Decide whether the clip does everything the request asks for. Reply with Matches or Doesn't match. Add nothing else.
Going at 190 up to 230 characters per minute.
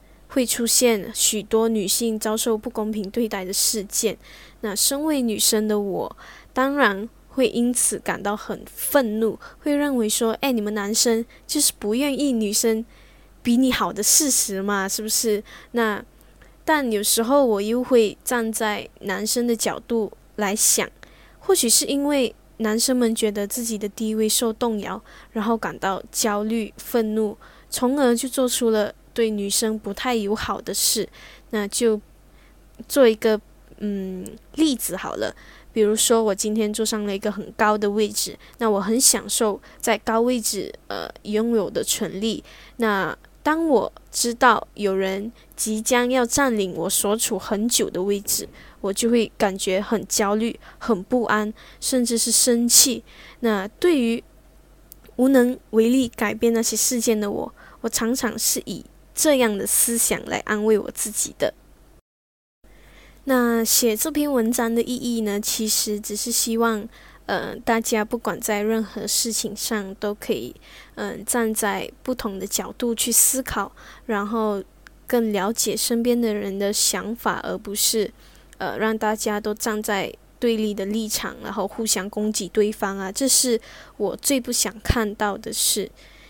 Matches